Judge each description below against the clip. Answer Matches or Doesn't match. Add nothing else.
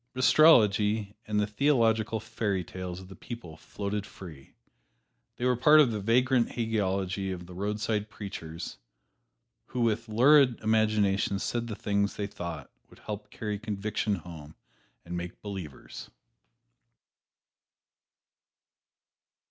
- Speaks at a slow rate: Matches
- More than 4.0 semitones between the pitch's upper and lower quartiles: Doesn't match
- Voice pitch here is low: Matches